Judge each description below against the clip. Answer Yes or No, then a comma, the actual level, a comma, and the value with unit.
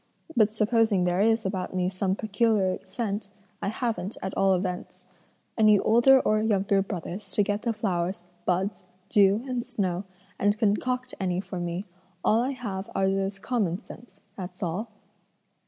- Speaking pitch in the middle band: No, high, 200 Hz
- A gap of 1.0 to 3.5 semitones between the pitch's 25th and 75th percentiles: Yes, average, 2.9 semitones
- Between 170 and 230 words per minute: No, average, 155 wpm